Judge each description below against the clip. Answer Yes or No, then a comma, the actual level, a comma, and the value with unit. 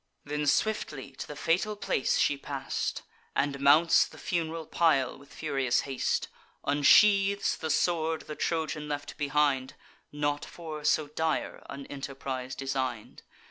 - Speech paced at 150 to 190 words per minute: No, slow, 135 wpm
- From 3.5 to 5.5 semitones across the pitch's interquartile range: No, average, 2.7 semitones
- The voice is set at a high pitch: No, medium, 145 Hz